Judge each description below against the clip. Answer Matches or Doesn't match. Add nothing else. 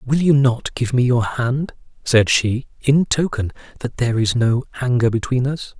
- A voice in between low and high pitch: Doesn't match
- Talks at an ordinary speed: Matches